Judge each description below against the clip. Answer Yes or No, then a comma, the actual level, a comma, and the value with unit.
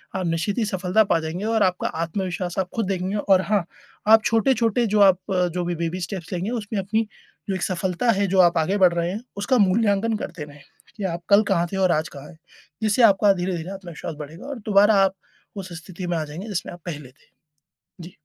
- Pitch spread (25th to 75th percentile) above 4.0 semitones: No, average, 3.1 semitones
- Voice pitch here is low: No, high, 190 Hz